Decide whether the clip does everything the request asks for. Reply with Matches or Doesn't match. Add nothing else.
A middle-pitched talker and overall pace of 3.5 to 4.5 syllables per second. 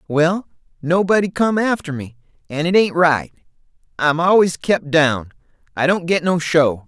Matches